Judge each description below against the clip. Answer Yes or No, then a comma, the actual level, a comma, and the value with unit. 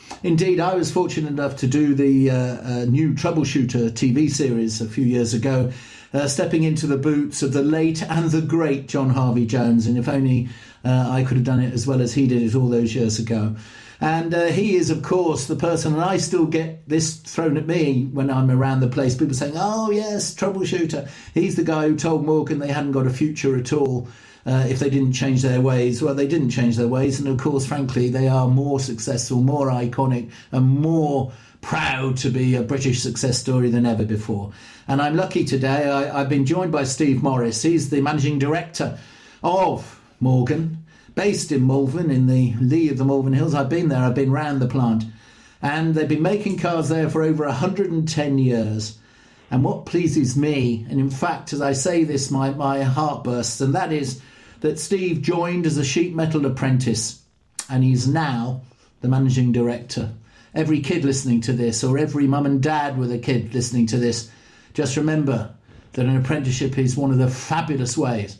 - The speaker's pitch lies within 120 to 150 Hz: Yes, low, 135 Hz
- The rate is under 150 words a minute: No, average, 200 wpm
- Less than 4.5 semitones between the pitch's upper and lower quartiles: Yes, average, 3.6 semitones